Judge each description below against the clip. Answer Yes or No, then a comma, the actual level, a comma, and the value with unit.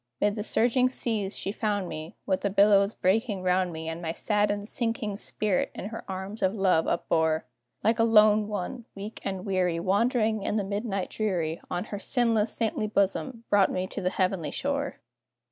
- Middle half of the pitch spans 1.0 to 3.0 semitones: Yes, average, 2.7 semitones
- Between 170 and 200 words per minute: Yes, average, 180 wpm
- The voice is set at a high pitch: Yes, high, 205 Hz